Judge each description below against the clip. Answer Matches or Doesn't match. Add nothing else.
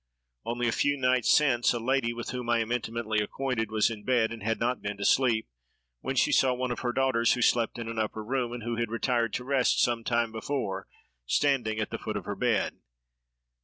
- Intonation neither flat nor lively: Doesn't match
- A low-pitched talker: Matches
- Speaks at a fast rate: Matches